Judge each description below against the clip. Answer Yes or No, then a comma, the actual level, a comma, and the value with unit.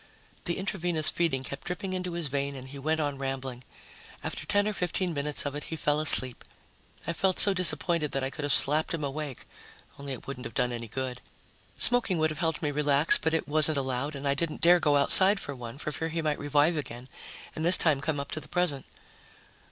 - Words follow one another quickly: Yes, fast, 220 wpm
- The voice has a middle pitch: Yes, medium, 150 Hz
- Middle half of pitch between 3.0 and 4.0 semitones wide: Yes, average, 3.3 semitones